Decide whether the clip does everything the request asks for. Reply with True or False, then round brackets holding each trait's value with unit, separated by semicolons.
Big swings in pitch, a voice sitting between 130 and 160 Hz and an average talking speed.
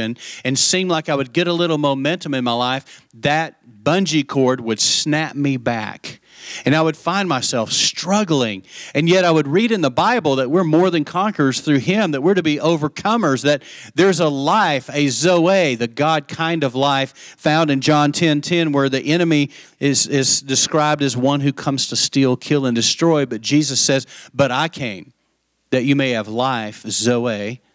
False (3.9 semitones; 140 Hz; 190 wpm)